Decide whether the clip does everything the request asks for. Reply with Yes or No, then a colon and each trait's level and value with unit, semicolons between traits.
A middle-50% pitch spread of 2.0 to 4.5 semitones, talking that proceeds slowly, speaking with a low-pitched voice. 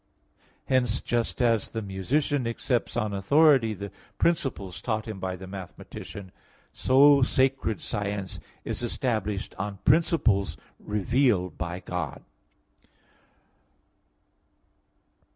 No: average, 5.0 semitones; slow, 100 wpm; low, 110 Hz